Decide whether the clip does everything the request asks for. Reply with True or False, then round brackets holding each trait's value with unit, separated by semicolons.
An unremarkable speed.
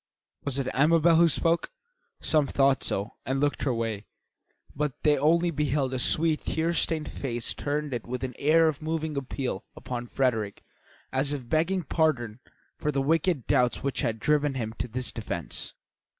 True (165 wpm)